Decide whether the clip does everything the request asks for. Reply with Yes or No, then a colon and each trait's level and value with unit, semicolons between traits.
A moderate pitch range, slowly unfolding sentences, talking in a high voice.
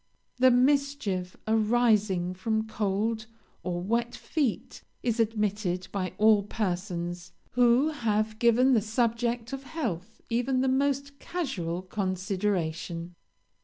Yes: average, 4.7 semitones; slow, 110 wpm; high, 220 Hz